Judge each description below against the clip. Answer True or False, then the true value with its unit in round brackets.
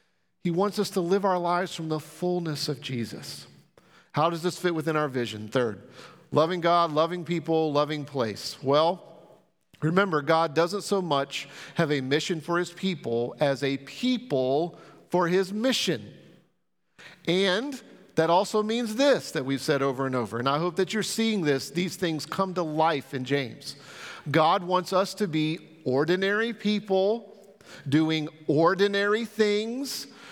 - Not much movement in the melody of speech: False (4.8 semitones)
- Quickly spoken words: False (155 wpm)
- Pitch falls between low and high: True (170 Hz)